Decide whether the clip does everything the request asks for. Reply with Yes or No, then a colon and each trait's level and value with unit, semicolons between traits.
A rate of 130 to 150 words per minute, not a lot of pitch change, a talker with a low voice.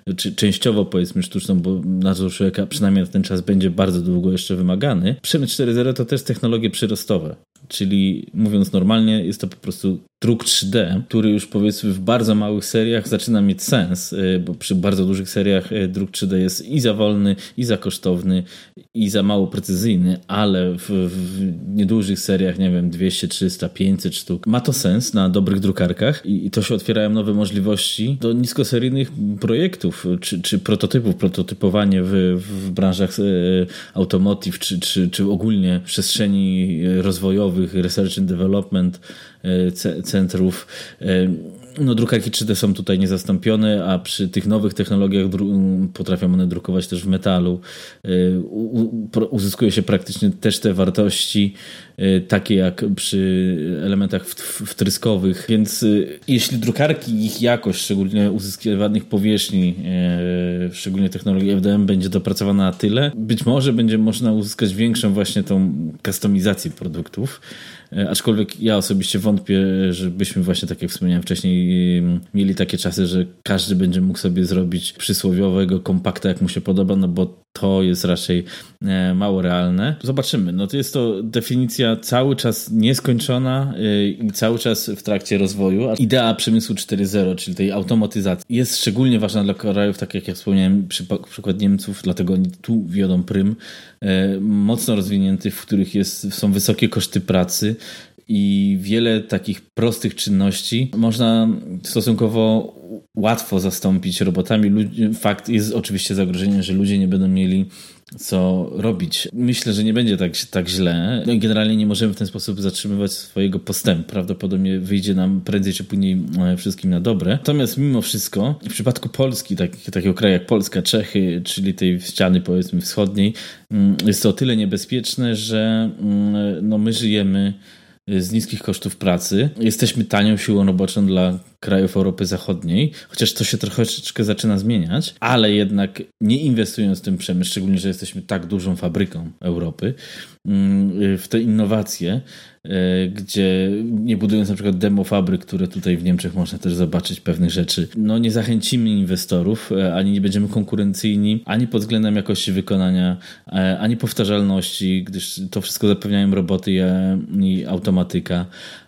No: average, 145 wpm; average, 3.0 semitones; low, 100 Hz